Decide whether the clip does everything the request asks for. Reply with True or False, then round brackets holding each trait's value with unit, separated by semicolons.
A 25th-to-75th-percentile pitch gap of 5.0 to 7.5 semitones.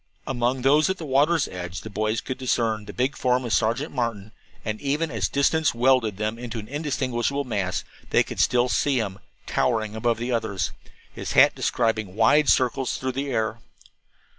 False (3.7 semitones)